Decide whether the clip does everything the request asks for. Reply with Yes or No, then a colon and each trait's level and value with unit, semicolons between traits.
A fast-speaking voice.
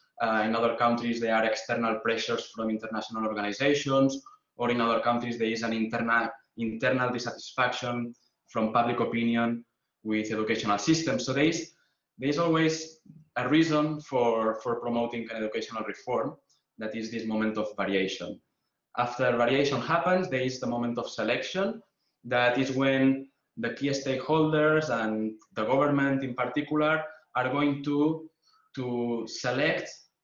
No: average, 145 wpm